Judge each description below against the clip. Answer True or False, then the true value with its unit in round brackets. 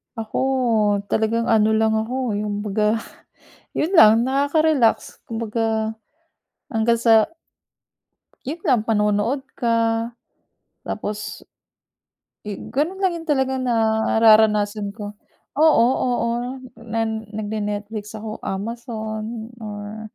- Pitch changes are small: True (2.0 semitones)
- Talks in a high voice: True (225 Hz)